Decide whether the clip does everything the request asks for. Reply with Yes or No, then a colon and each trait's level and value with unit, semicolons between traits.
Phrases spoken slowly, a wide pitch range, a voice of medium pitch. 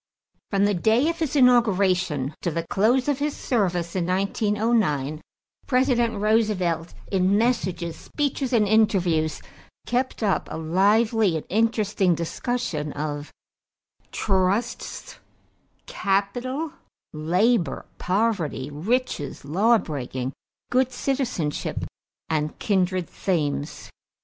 No: slow, 100 wpm; wide, 6.0 semitones; high, 200 Hz